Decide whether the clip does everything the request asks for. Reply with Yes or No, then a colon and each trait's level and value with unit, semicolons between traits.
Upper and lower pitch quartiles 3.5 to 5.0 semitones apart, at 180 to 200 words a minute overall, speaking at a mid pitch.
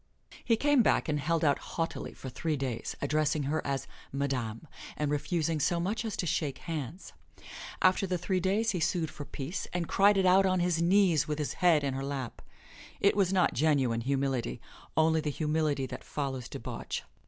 Yes: average, 4.4 semitones; average, 190 wpm; medium, 155 Hz